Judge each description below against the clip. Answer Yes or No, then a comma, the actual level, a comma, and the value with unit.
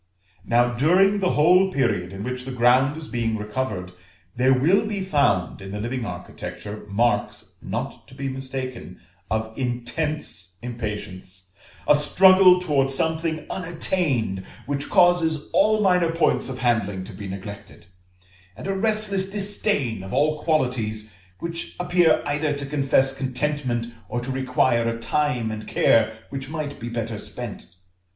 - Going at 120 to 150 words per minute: Yes, average, 145 wpm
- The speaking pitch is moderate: No, low, 130 Hz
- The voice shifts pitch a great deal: Yes, wide, 6.1 semitones